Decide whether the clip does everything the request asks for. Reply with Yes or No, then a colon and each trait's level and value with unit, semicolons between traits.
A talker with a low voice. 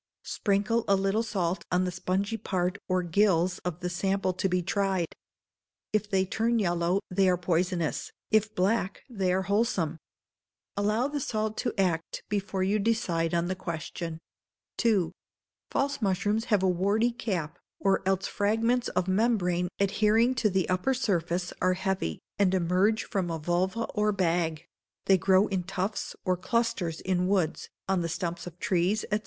No: high, 190 Hz